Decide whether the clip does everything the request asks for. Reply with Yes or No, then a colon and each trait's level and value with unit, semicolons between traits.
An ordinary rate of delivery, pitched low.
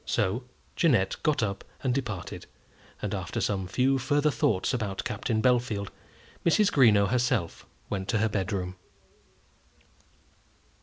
No: slow, 120 wpm; low, 110 Hz